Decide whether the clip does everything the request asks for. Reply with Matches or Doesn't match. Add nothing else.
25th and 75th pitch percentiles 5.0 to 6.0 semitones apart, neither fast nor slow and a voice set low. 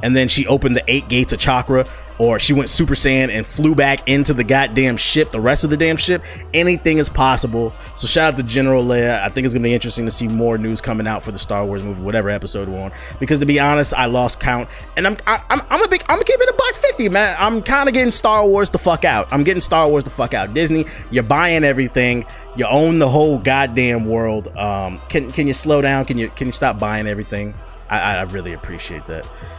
Doesn't match